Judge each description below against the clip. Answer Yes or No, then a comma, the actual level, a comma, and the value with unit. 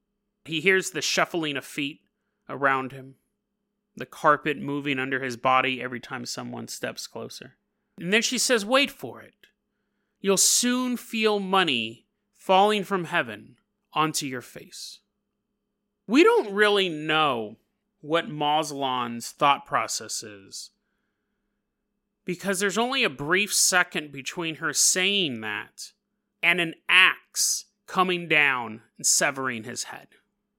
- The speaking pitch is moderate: Yes, medium, 180 Hz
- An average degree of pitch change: No, wide, 7.1 semitones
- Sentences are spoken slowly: Yes, slow, 125 wpm